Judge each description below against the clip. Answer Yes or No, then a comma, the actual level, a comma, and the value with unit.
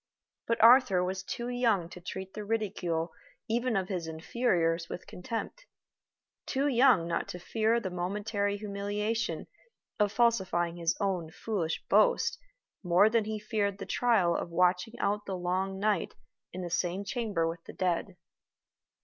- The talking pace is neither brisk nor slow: Yes, average, 150 wpm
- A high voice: Yes, high, 200 Hz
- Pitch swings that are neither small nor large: Yes, average, 4.0 semitones